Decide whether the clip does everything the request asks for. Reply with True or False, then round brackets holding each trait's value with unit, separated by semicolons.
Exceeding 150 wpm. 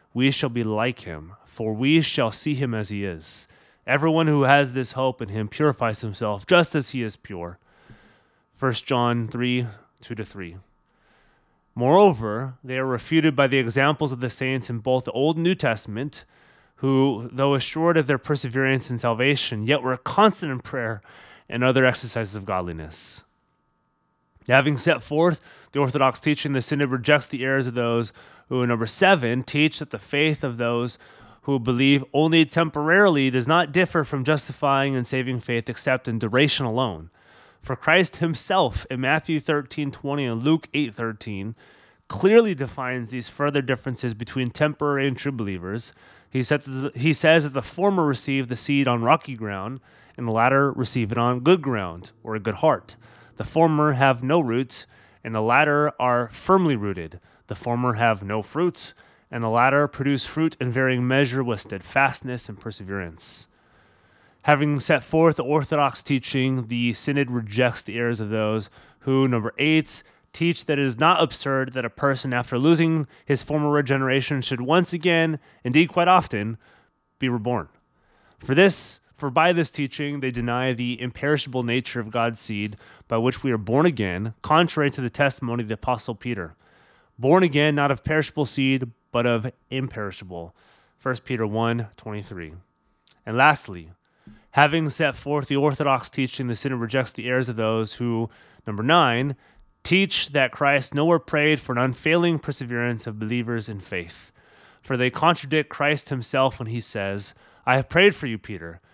True (170 wpm)